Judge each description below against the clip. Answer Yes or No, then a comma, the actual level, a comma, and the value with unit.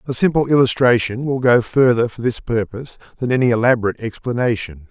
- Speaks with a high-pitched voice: No, low, 120 Hz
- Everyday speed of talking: Yes, average, 160 wpm